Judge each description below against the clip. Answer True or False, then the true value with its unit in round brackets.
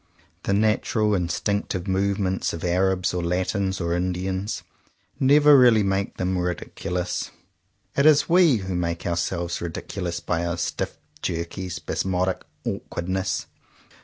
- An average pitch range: False (2.3 semitones)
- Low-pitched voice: True (95 Hz)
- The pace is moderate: False (120 wpm)